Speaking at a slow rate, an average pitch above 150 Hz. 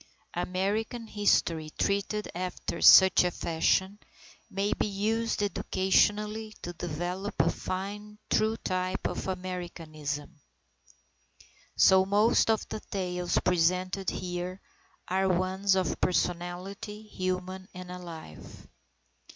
Yes: slow, 100 wpm; medium, 185 Hz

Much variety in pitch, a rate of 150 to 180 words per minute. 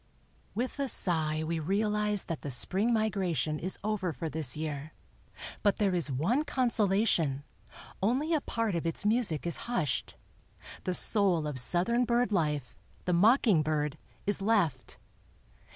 No: wide, 5.8 semitones; average, 140 wpm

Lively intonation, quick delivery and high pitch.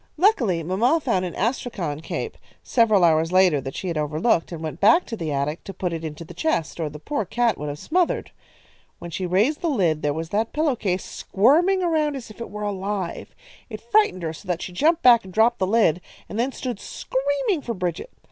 Yes: wide, 7.3 semitones; fast, 220 wpm; high, 200 Hz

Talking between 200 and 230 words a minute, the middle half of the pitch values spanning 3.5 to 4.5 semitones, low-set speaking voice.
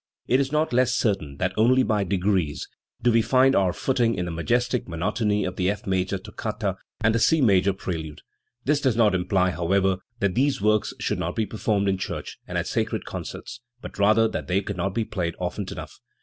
Yes: fast, 205 wpm; average, 4.1 semitones; low, 100 Hz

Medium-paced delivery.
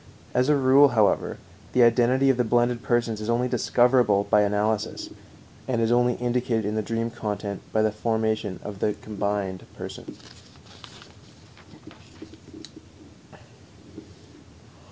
No: slow, 120 wpm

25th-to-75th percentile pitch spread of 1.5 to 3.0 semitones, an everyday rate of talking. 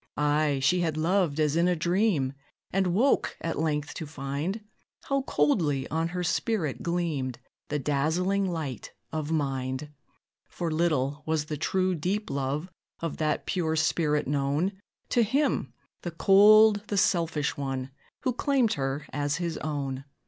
No: average, 3.9 semitones; average, 150 wpm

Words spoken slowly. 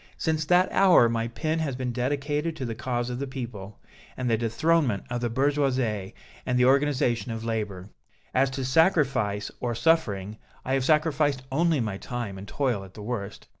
No: average, 175 wpm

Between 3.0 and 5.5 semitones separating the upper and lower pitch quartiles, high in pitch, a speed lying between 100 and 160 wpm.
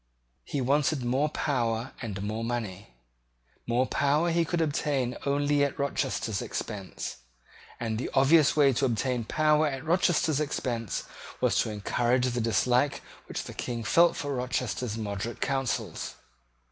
No: average, 3.9 semitones; low, 130 Hz; average, 140 wpm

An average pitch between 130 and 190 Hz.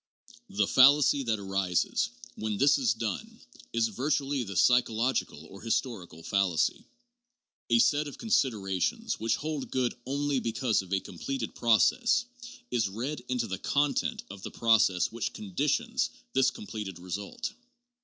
No: low, 115 Hz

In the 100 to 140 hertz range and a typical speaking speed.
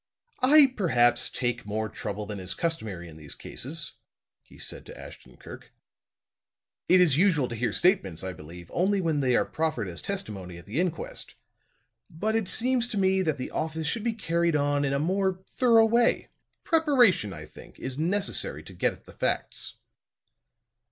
No: medium, 160 Hz; average, 175 wpm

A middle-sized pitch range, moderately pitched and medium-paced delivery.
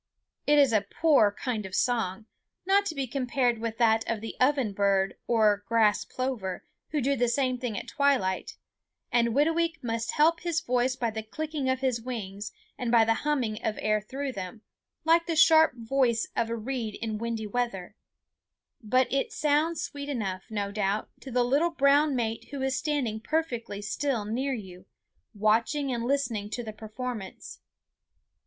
No: average, 4.5 semitones; high, 240 Hz; average, 175 wpm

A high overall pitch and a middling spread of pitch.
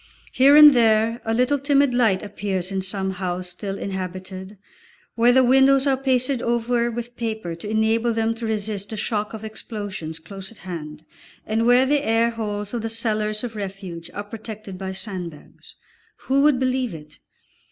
Yes: high, 220 Hz; average, 4.0 semitones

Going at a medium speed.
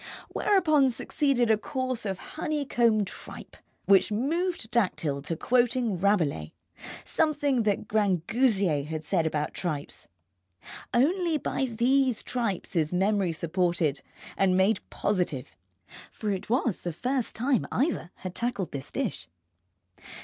No: slow, 120 wpm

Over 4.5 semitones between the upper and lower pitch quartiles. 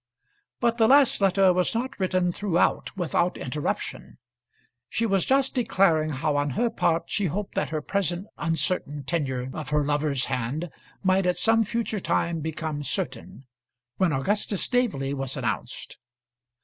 Yes: wide, 5.6 semitones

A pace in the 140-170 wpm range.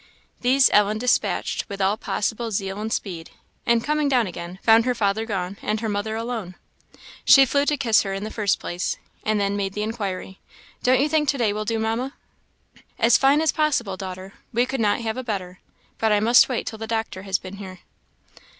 No: fast, 205 wpm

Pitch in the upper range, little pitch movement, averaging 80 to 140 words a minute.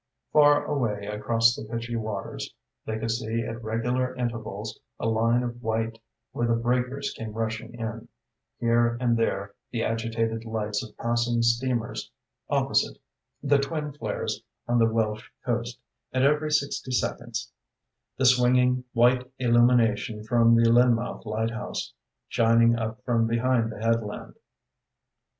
No: low, 115 Hz; narrow, 1.6 semitones; slow, 135 wpm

